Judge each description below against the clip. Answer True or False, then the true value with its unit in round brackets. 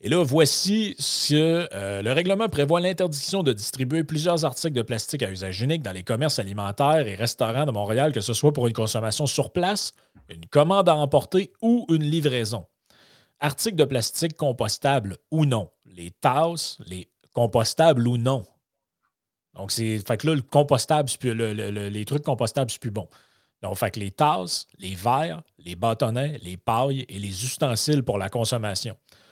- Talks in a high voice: False (130 Hz)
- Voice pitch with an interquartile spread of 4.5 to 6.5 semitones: True (5.6 semitones)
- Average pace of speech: True (170 wpm)